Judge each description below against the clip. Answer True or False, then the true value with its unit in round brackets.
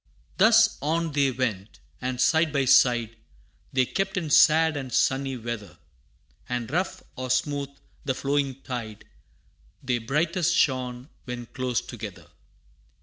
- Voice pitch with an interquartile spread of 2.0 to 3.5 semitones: False (3.9 semitones)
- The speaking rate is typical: False (130 wpm)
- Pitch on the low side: True (130 Hz)